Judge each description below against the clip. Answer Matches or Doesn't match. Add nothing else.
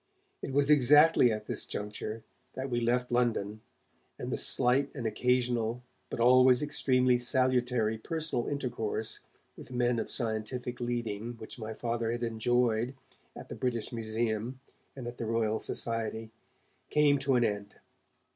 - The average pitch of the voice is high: Doesn't match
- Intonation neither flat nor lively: Doesn't match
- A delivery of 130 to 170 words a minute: Matches